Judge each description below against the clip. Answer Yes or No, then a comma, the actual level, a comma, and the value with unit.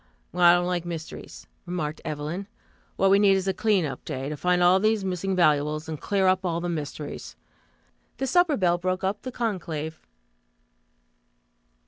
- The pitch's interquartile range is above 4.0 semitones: No, average, 3.4 semitones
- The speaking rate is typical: Yes, average, 170 wpm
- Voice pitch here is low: No, medium, 180 Hz